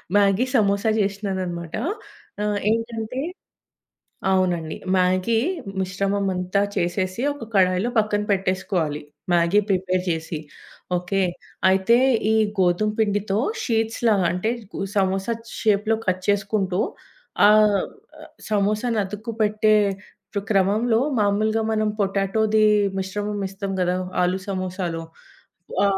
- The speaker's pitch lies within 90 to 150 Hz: No, high, 200 Hz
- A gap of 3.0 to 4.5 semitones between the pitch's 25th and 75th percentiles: No, narrow, 2.5 semitones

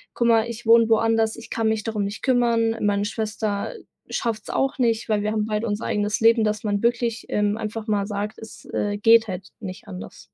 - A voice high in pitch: Yes, high, 220 Hz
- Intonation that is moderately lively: No, narrow, 1.7 semitones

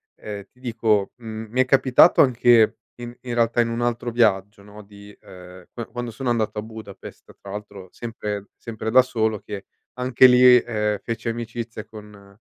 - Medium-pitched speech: No, low, 110 Hz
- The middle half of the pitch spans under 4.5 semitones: Yes, narrow, 2.4 semitones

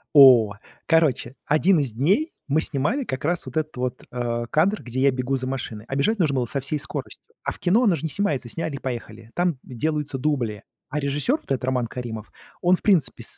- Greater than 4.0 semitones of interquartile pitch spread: Yes, average, 4.5 semitones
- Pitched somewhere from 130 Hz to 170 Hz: Yes, medium, 140 Hz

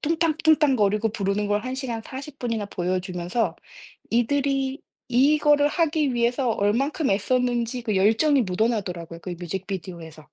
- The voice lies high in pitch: Yes, high, 235 Hz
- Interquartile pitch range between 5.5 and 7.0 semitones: Yes, wide, 5.8 semitones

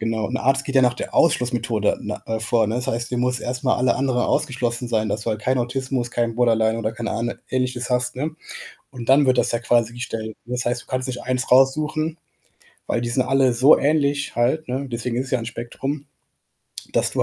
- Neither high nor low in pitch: No, low, 125 Hz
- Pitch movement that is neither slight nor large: No, narrow, 2.0 semitones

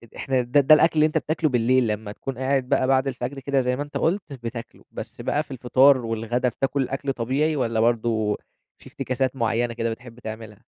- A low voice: Yes, low, 130 Hz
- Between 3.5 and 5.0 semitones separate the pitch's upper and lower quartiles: No, average, 2.9 semitones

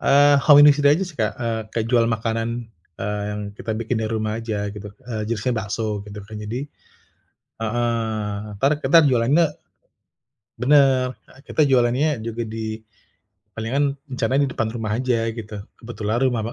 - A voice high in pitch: No, low, 115 Hz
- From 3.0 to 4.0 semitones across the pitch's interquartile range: Yes, average, 3.3 semitones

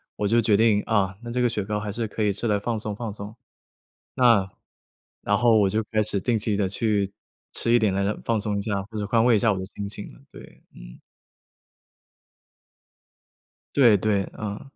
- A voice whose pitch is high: No, low, 105 Hz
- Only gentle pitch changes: Yes, narrow, 2.1 semitones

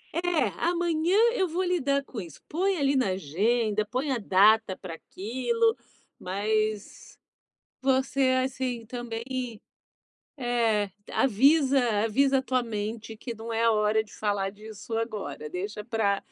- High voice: Yes, high, 230 Hz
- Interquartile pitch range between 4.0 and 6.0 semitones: Yes, average, 4.4 semitones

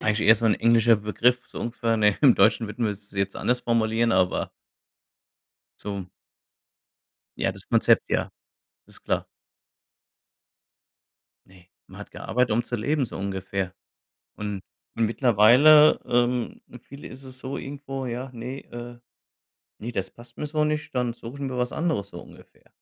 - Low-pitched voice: Yes, low, 120 Hz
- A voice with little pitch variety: No, average, 3.3 semitones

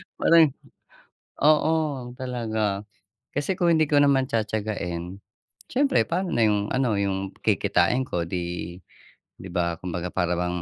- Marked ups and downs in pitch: Yes, wide, 7.7 semitones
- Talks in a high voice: No, low, 105 Hz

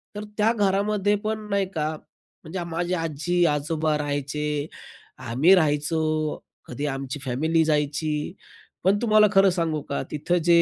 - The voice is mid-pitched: Yes, medium, 160 Hz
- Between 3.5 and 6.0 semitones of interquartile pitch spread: Yes, average, 4.5 semitones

